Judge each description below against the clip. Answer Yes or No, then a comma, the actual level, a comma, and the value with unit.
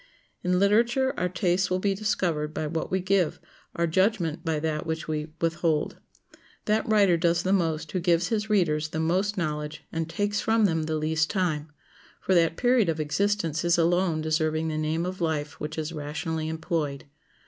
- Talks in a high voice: No, medium, 165 Hz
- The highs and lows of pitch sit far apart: No, average, 3.2 semitones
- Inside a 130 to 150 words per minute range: No, average, 180 wpm